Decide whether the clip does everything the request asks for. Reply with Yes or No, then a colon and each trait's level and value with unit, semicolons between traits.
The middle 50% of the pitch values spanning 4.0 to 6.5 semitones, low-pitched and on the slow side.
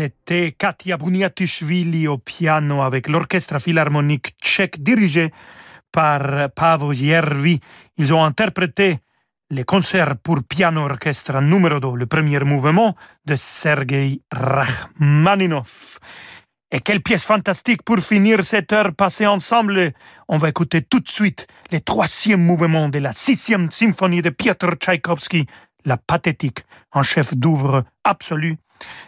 No: average, 4.6 semitones; medium, 165 Hz; slow, 125 wpm